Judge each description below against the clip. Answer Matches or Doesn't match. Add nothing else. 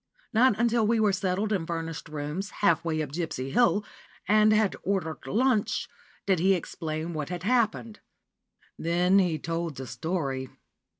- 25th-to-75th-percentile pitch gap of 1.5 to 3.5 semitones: Doesn't match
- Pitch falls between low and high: Matches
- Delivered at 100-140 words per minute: Doesn't match